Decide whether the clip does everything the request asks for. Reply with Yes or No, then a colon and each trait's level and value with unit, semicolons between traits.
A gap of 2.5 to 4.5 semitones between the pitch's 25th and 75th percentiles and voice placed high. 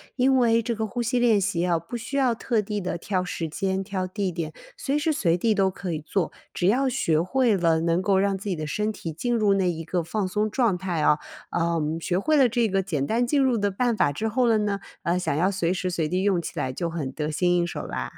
No: average, 4.9 semitones; high, 195 Hz